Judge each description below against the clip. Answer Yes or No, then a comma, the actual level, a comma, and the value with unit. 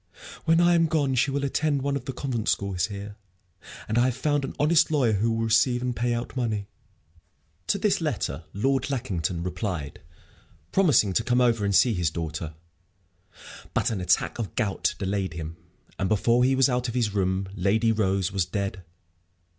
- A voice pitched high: No, low, 115 Hz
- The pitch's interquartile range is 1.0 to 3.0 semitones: No, average, 5.2 semitones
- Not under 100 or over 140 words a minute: No, average, 185 wpm